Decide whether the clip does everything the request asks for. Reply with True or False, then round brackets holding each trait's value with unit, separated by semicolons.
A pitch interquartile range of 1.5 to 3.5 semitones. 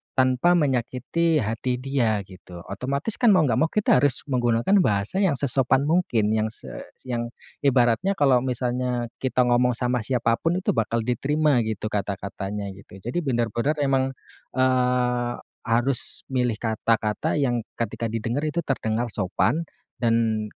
True (3.2 semitones)